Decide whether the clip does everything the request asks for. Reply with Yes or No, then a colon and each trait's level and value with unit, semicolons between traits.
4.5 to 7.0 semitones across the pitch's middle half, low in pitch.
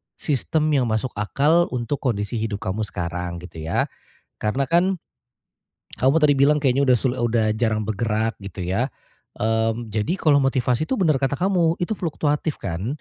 Yes: wide, 5.4 semitones; low, 125 Hz